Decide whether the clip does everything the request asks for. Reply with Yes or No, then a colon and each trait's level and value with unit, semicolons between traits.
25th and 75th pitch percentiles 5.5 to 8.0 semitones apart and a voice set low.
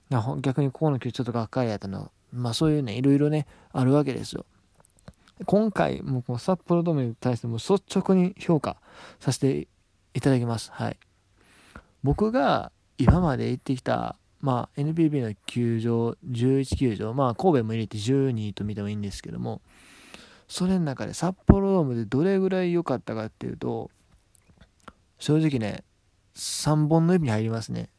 Yes: wide, 5.8 semitones; low, 130 Hz